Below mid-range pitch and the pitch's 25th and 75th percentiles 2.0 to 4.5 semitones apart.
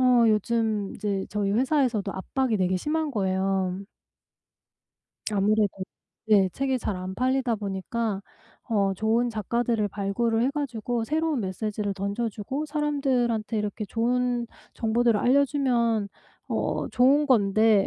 No: high, 225 Hz; average, 3.7 semitones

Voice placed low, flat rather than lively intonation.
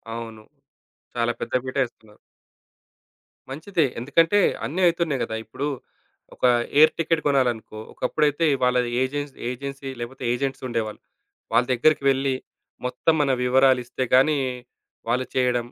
No: low, 130 Hz; average, 3.1 semitones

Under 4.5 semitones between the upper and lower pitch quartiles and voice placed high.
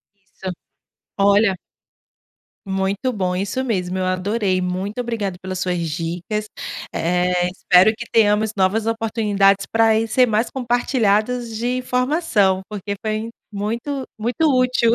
Yes: average, 3.4 semitones; high, 210 Hz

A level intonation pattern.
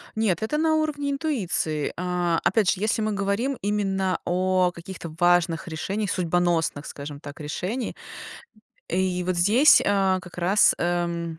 No: average, 3.4 semitones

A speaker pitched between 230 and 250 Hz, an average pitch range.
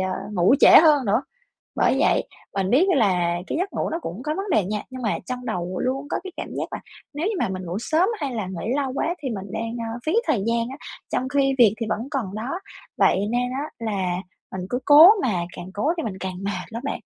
No: high, 235 Hz; wide, 6.5 semitones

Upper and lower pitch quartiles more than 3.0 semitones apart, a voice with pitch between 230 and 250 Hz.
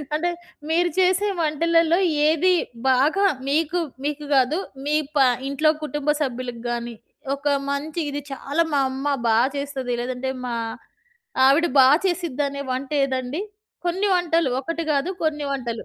No: average, 3.9 semitones; very high, 290 Hz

